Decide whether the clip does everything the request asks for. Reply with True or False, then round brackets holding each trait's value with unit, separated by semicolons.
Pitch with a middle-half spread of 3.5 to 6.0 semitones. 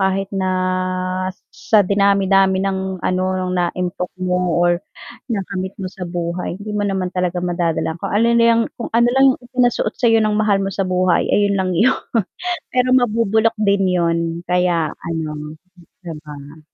False (2.9 semitones)